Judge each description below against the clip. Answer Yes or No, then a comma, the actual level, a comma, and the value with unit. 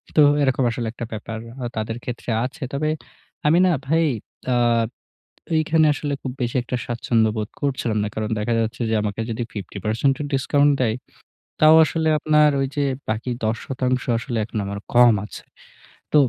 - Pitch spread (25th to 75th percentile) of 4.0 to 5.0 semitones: Yes, average, 4.3 semitones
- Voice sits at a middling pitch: No, low, 120 Hz